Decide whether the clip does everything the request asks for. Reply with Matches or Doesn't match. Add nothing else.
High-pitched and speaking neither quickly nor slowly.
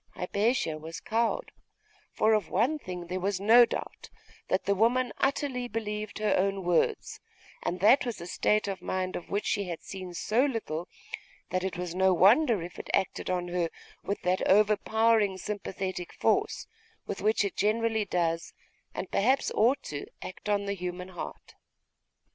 Matches